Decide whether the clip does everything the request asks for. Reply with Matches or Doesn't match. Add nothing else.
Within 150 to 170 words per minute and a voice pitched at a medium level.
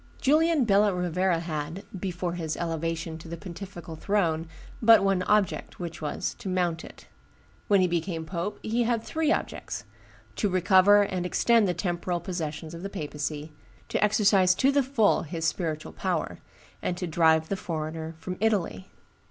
Matches